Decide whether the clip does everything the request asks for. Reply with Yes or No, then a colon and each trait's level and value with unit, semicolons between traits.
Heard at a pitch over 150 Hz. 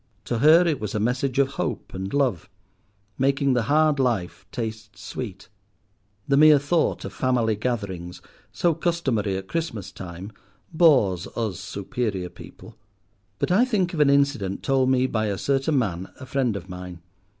No: low, 125 Hz